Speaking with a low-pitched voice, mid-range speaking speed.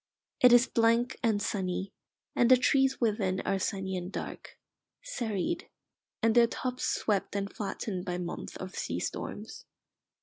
No: high, 210 Hz; average, 145 wpm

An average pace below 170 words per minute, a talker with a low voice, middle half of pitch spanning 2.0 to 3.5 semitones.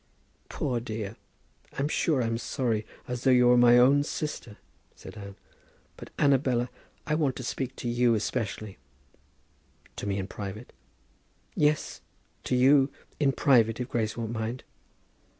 Yes: average, 145 wpm; low, 120 Hz; average, 3.2 semitones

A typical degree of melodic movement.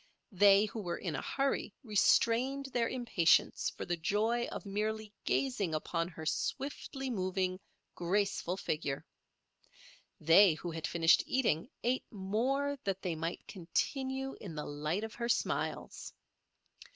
No: wide, 5.8 semitones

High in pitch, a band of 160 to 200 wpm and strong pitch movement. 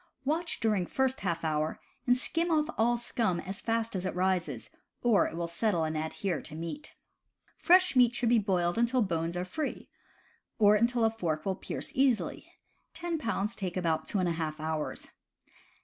Yes: high, 200 Hz; average, 180 wpm; wide, 6.2 semitones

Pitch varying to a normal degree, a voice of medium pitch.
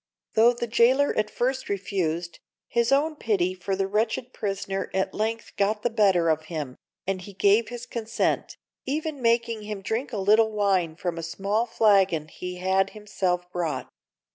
No: average, 4.0 semitones; high, 205 Hz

